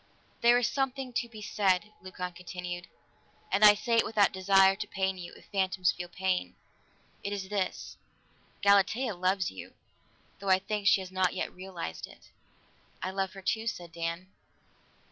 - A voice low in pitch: No, high, 190 Hz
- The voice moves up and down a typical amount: No, narrow, 2.3 semitones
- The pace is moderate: Yes, average, 165 wpm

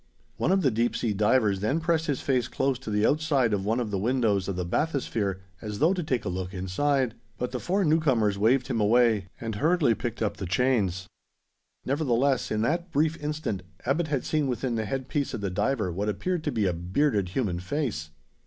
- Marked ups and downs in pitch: Yes, wide, 5.8 semitones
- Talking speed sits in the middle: No, fast, 210 wpm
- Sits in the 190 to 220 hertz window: No, low, 120 Hz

